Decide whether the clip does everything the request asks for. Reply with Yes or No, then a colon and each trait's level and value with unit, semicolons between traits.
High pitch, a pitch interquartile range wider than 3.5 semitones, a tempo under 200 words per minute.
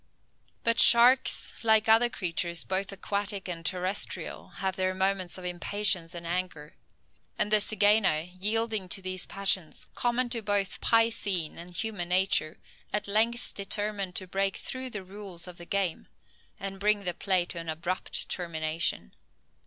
No: high, 195 Hz; average, 2.9 semitones; average, 150 wpm